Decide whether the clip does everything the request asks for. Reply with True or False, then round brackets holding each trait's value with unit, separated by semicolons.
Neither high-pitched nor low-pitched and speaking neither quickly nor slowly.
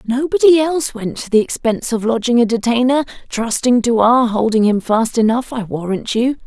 False (240 Hz; 185 wpm)